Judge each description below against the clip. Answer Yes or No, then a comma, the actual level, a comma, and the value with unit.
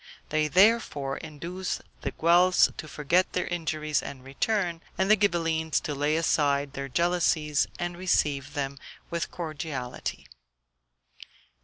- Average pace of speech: No, slow, 125 wpm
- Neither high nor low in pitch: Yes, medium, 160 Hz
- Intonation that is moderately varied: Yes, average, 3.4 semitones